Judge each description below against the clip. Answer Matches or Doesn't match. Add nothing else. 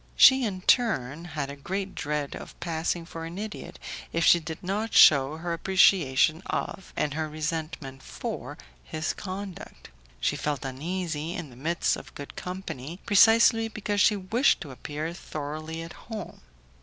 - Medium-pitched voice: Matches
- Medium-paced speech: Matches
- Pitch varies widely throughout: Doesn't match